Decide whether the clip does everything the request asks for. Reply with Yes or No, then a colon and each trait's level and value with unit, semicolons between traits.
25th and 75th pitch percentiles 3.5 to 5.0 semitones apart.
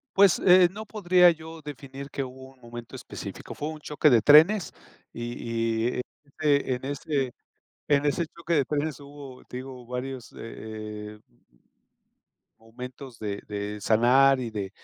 Yes: average, 4.1 semitones